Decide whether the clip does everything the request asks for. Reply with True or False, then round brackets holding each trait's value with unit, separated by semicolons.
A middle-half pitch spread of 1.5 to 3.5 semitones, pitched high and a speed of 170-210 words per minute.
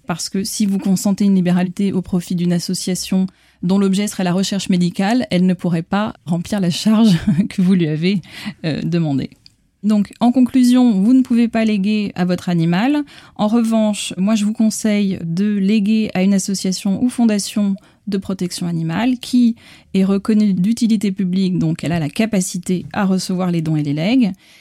True (2.9 semitones; 195 Hz; 180 wpm)